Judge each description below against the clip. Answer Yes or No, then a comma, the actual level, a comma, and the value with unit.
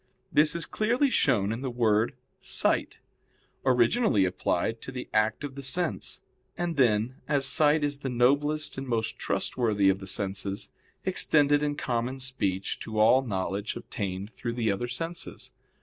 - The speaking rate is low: No, average, 155 wpm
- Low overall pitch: Yes, low, 125 Hz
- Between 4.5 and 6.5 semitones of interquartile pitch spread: Yes, average, 5.2 semitones